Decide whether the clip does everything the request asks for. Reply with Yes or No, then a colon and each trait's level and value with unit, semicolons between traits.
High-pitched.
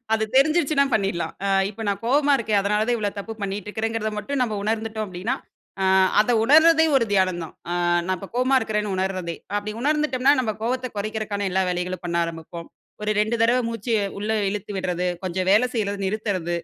Yes: high, 215 Hz